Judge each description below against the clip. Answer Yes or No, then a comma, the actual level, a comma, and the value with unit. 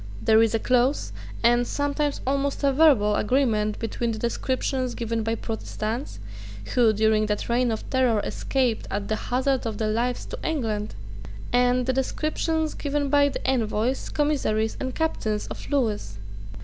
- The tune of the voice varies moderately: Yes, average, 3.8 semitones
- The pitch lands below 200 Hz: No, high, 245 Hz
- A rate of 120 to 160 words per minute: Yes, average, 155 wpm